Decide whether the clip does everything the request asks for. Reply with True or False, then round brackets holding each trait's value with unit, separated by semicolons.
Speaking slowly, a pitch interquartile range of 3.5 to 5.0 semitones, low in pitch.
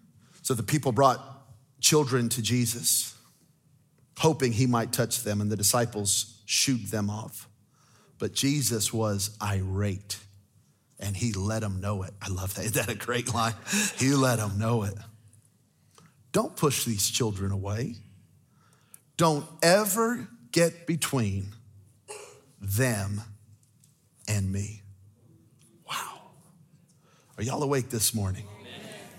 True (120 wpm; 4.6 semitones; 115 Hz)